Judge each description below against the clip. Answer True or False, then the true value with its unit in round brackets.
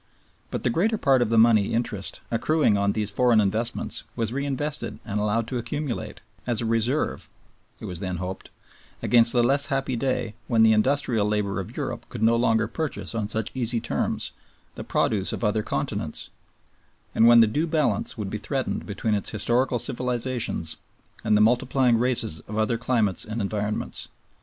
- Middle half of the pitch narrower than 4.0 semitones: True (2.9 semitones)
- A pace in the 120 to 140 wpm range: False (175 wpm)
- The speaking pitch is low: True (115 Hz)